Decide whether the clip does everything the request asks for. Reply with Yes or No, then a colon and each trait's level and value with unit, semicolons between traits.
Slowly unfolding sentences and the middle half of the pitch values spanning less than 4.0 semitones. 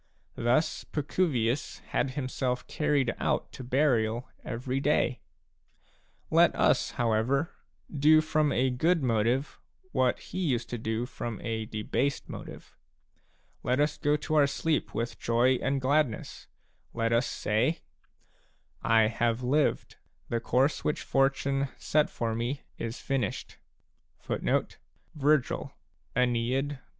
Yes: slow, 120 wpm; average, 3.6 semitones